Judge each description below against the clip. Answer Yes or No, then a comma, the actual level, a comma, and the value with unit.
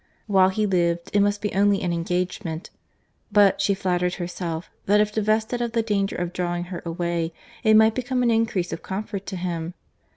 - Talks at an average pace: Yes, average, 190 wpm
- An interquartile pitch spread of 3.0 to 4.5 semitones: Yes, average, 3.3 semitones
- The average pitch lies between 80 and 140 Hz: No, high, 190 Hz